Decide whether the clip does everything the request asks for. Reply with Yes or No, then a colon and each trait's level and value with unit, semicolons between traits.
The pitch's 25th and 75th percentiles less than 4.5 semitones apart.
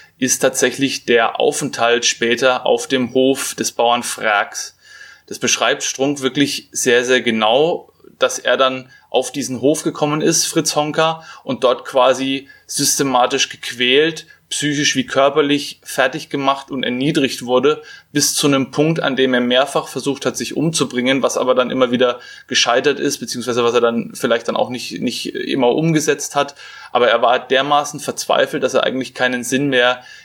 Yes: narrow, 2.6 semitones